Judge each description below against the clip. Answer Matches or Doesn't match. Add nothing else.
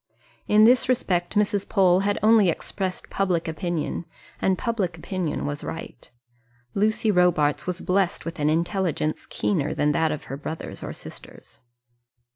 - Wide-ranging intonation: Doesn't match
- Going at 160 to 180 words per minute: Doesn't match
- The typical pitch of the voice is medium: Matches